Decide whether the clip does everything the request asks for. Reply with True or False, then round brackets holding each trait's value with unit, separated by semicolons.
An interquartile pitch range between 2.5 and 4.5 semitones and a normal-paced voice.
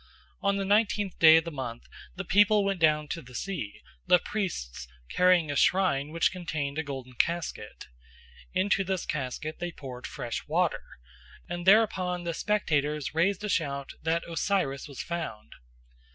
False (5.1 semitones; 155 wpm)